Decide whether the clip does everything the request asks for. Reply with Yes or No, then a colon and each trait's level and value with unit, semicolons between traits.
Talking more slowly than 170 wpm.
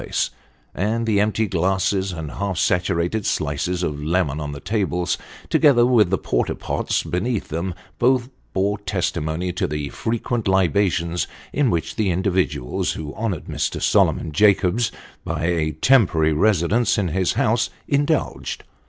Yes: average, 140 wpm